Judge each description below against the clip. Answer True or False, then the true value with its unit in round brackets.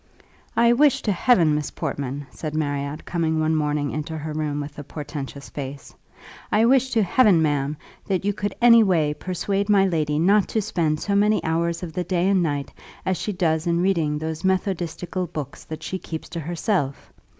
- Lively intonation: False (4.4 semitones)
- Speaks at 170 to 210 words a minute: True (190 wpm)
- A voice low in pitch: False (165 Hz)